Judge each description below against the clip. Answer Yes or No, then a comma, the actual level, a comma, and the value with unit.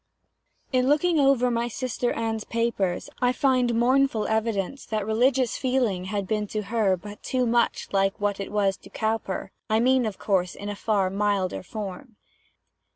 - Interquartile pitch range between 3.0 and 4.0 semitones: Yes, average, 3.7 semitones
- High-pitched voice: Yes, high, 220 Hz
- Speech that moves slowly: No, average, 165 wpm